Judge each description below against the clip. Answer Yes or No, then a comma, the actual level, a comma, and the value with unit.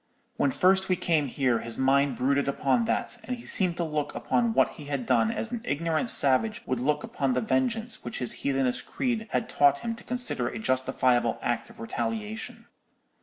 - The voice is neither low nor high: Yes, medium, 150 Hz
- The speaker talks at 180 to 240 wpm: Yes, average, 195 wpm